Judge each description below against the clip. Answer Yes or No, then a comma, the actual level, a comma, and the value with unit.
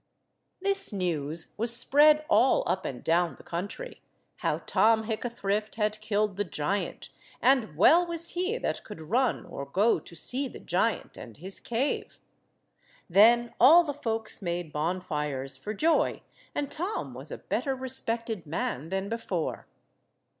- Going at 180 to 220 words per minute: No, average, 145 wpm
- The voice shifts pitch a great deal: Yes, wide, 7.2 semitones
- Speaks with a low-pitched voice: No, high, 215 Hz